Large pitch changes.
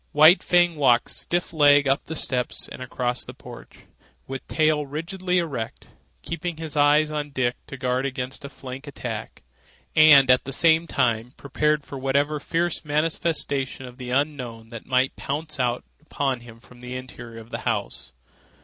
No: average, 3.4 semitones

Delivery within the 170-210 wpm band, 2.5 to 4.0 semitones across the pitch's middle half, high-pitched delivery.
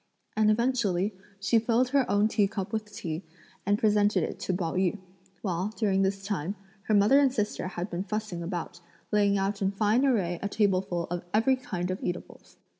Yes: average, 190 wpm; average, 2.8 semitones; high, 200 Hz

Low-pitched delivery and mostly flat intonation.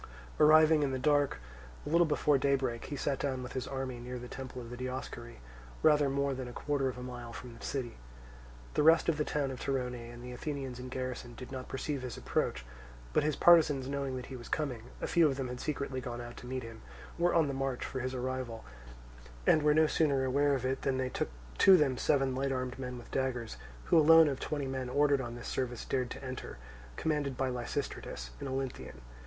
Yes: low, 130 Hz; narrow, 2.3 semitones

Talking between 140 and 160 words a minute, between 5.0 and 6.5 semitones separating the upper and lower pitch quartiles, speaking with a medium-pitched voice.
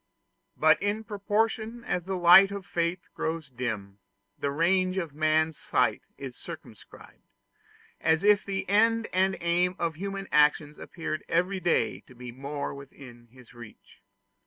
Yes: average, 145 wpm; wide, 5.5 semitones; medium, 170 Hz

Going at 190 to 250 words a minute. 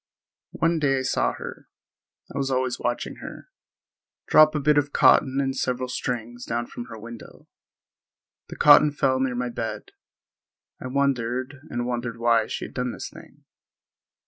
No: average, 150 wpm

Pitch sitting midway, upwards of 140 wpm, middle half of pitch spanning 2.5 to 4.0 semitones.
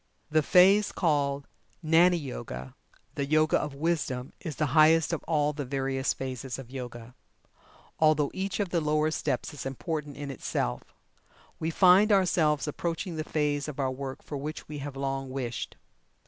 Yes: medium, 150 Hz; average, 160 wpm; average, 3.1 semitones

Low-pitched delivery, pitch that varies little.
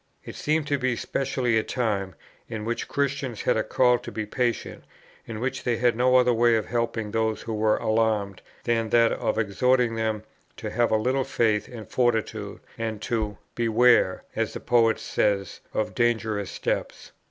Yes: low, 115 Hz; narrow, 2.1 semitones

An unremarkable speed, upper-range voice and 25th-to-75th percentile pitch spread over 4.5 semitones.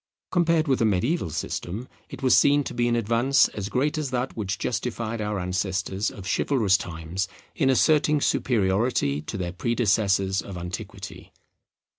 No: average, 155 wpm; low, 110 Hz; wide, 5.5 semitones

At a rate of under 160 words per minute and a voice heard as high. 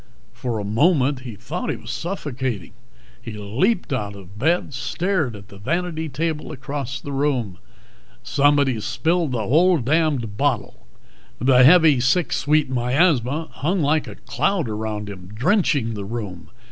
No: average, 150 wpm; low, 130 Hz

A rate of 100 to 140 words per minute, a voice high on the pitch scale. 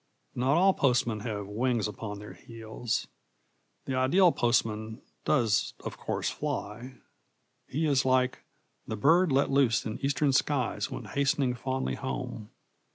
No: slow, 135 wpm; low, 125 Hz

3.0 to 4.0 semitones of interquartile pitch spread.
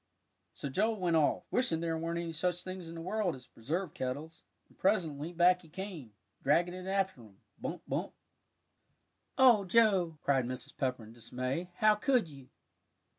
No: average, 5.1 semitones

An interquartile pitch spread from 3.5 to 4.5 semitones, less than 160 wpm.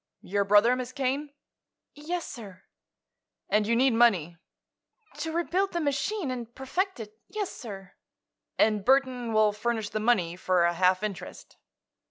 No: average, 5.1 semitones; average, 145 wpm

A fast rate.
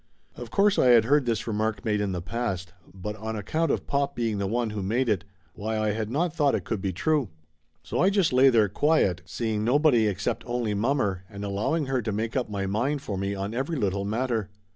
Yes: fast, 230 wpm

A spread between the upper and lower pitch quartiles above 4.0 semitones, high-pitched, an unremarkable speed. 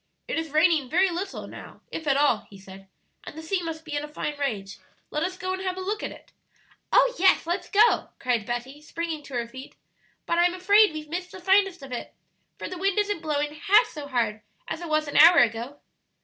No: average, 5.0 semitones; very high, 315 Hz; fast, 230 wpm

